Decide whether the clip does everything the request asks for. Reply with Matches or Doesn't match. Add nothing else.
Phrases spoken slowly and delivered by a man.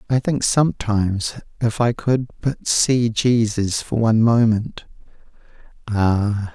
Matches